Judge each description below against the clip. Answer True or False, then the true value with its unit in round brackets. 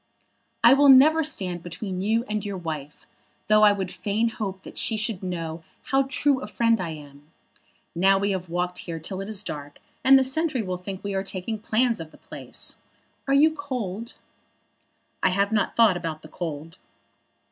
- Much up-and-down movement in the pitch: False (4.7 semitones)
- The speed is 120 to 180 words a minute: False (190 wpm)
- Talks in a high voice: True (195 Hz)